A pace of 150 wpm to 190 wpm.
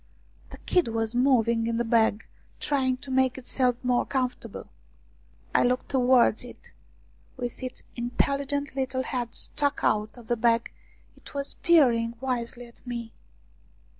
No: average, 140 wpm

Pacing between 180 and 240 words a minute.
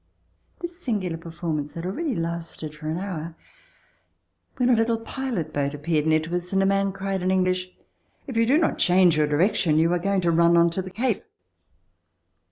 Yes: average, 190 wpm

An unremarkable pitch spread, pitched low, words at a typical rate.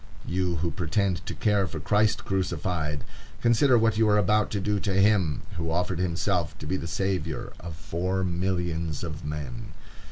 Yes: average, 3.4 semitones; very low, 90 Hz; average, 170 wpm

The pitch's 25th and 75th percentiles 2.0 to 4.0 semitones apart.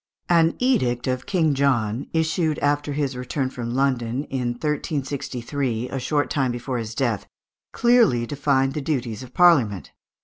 Yes: average, 3.5 semitones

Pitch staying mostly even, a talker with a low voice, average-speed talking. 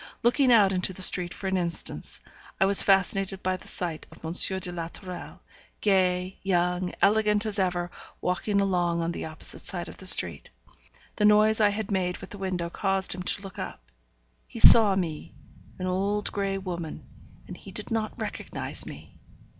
No: narrow, 2.2 semitones; high, 190 Hz; average, 180 wpm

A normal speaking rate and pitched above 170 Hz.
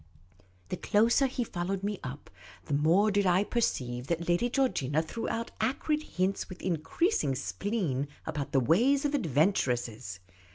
Yes: average, 150 wpm; medium, 185 Hz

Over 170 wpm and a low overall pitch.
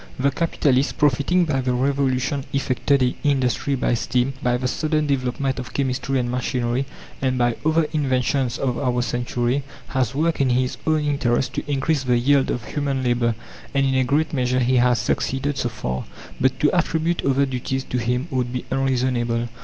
Yes: average, 180 wpm; low, 130 Hz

